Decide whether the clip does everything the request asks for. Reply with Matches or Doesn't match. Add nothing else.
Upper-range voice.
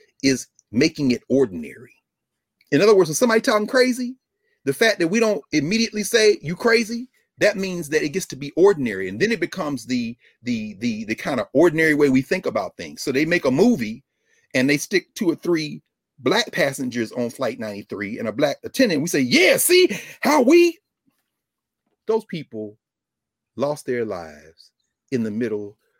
Doesn't match